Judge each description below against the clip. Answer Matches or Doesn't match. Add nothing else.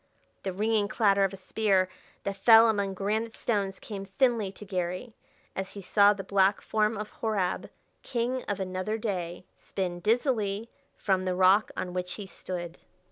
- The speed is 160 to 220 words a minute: Matches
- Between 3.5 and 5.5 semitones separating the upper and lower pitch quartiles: Doesn't match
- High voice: Matches